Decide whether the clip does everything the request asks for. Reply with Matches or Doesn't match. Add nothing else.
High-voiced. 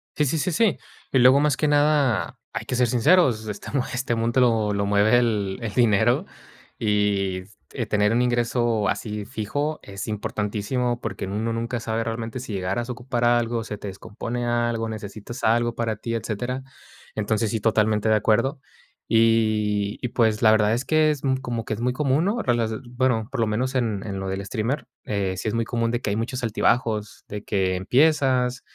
Doesn't match